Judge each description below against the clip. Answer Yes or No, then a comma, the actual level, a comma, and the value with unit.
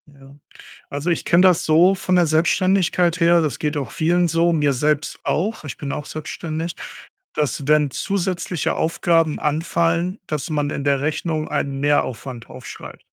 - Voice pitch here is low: No, medium, 160 Hz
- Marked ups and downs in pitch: No, average, 2.8 semitones